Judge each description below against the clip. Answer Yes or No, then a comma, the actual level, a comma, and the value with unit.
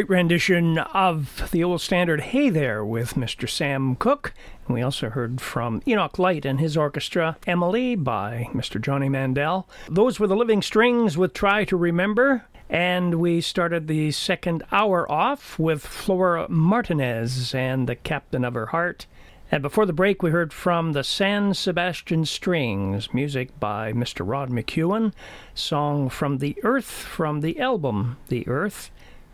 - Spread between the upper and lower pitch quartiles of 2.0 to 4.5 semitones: No, wide, 5.6 semitones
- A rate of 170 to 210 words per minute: No, average, 155 wpm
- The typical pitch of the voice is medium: Yes, medium, 165 Hz